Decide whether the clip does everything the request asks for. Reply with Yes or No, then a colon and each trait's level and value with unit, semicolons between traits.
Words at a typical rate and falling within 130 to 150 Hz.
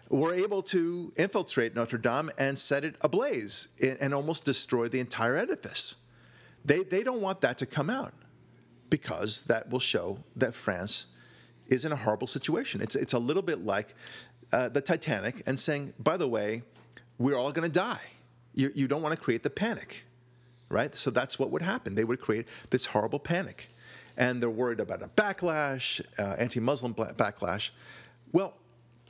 Yes: average, 175 wpm; low, 135 Hz